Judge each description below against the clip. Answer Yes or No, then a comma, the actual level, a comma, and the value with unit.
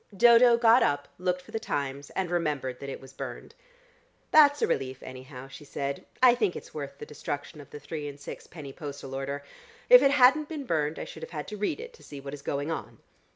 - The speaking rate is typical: No, fast, 225 wpm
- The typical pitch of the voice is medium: Yes, medium, 150 Hz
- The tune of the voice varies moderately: No, wide, 8.9 semitones